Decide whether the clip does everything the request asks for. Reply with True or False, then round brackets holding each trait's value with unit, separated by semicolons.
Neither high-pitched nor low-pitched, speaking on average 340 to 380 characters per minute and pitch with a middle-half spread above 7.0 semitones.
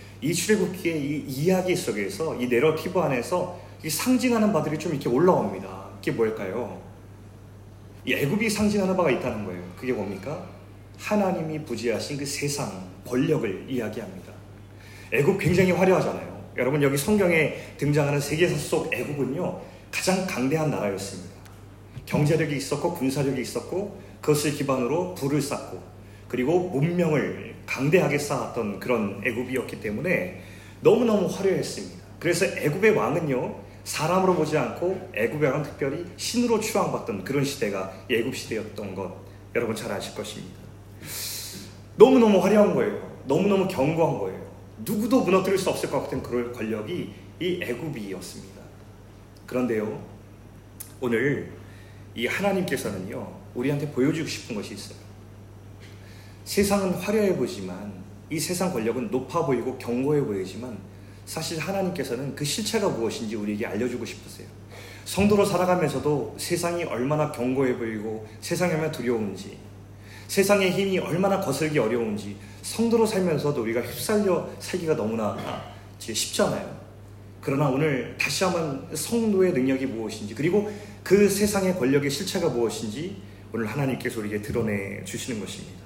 False (125 Hz; 345 characters per minute; 8.8 semitones)